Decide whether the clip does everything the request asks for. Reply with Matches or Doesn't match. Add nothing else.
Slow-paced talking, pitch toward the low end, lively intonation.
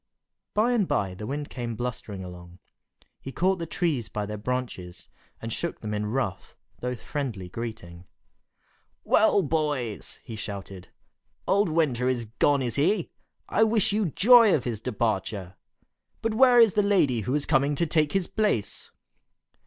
Doesn't match